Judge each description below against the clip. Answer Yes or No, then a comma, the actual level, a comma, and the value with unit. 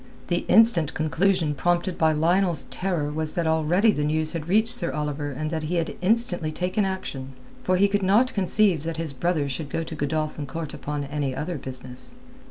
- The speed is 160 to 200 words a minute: Yes, average, 190 wpm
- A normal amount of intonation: Yes, average, 3.6 semitones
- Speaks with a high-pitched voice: No, medium, 160 Hz